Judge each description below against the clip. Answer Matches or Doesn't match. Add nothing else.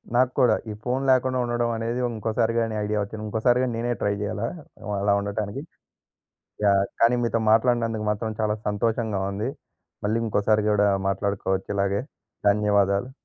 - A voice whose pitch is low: Matches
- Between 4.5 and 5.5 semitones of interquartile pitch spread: Doesn't match